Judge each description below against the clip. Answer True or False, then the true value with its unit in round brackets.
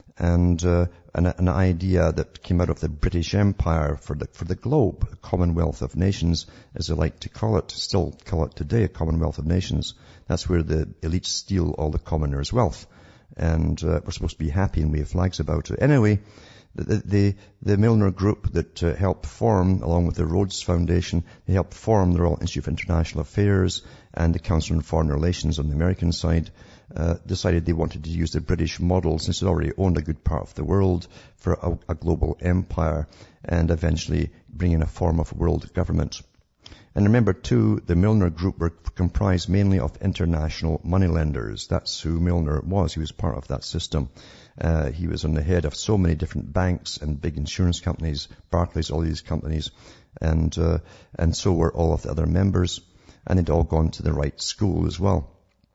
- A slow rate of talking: False (200 wpm)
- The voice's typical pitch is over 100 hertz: False (85 Hz)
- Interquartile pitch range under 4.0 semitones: True (2.8 semitones)